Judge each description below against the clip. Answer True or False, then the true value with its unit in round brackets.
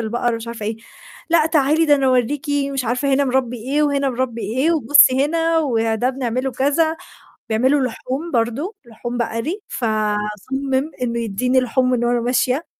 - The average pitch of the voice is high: True (255 Hz)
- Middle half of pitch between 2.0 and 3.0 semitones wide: False (3.4 semitones)